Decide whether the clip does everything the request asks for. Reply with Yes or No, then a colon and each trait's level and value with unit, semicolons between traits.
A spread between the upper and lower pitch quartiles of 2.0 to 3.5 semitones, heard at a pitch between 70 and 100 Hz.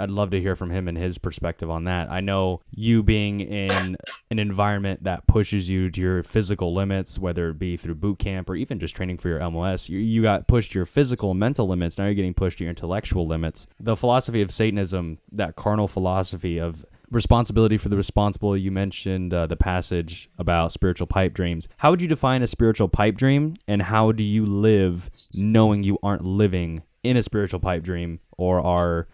Yes: average, 2.8 semitones; very low, 95 Hz